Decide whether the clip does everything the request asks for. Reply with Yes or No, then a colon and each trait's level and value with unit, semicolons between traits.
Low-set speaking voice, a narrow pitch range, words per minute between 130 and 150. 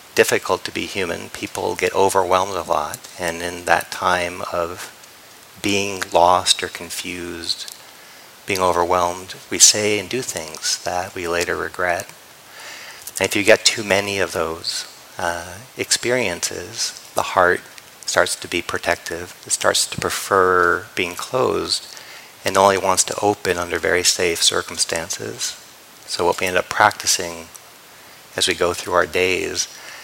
Yes: very low, 95 Hz; narrow, 2.3 semitones; average, 145 wpm